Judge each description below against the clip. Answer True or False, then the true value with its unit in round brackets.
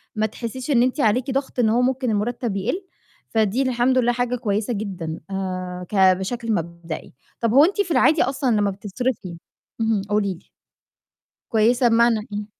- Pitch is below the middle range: False (225 Hz)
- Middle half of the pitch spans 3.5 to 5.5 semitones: True (4.0 semitones)